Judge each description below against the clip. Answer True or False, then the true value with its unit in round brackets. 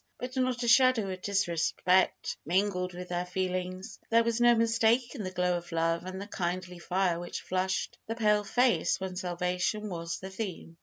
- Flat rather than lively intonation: False (3.9 semitones)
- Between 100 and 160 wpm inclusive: False (175 wpm)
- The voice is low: False (185 Hz)